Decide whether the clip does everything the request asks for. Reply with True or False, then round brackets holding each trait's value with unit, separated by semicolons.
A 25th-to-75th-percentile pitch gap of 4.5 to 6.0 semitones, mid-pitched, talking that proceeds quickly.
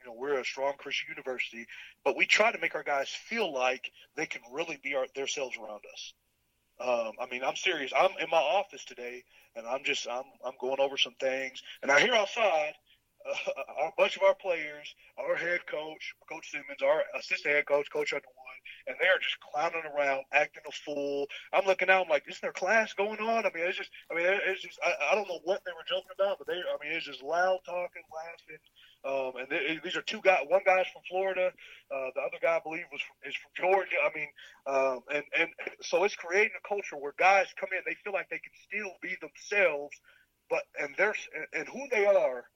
True (5.5 semitones; 170 Hz; 230 wpm)